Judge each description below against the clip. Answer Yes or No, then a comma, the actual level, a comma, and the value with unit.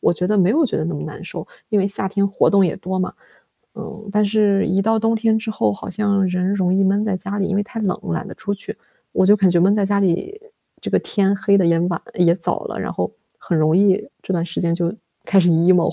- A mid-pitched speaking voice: No, high, 195 Hz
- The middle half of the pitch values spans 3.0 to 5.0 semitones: No, narrow, 2.5 semitones